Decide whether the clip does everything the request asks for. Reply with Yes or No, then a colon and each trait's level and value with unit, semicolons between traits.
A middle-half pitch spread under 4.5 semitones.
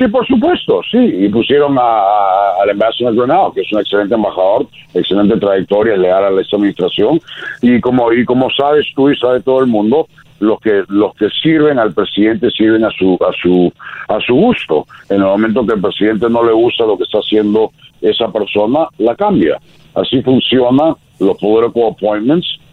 No: average, 4.8 semitones